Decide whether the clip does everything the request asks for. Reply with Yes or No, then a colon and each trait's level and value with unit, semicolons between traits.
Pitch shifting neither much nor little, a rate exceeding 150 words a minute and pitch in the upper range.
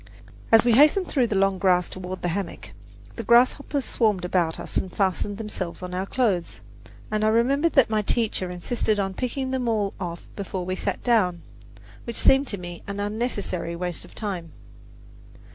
Yes: average, 4.6 semitones; average, 180 wpm; high, 200 Hz